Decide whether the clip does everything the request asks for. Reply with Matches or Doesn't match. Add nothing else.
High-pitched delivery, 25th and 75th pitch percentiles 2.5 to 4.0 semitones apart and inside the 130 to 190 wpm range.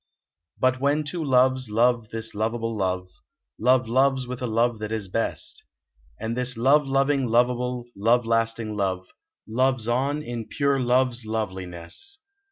Doesn't match